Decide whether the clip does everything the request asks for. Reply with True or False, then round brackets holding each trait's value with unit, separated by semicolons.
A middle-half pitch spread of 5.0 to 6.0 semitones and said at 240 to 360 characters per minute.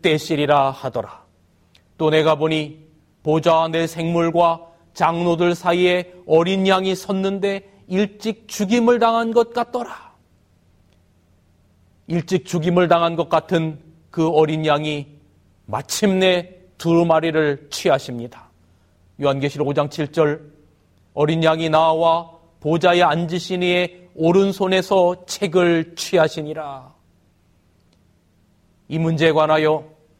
False (5.5 semitones; 215 characters per minute)